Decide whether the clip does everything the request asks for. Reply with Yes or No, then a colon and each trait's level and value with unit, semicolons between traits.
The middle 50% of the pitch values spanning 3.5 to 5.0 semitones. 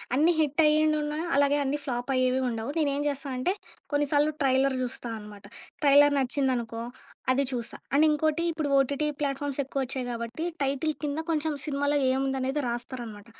No: narrow, 2.5 semitones